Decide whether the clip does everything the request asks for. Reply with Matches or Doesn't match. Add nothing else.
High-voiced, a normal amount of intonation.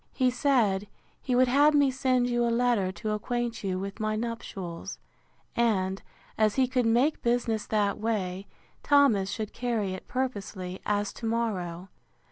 Matches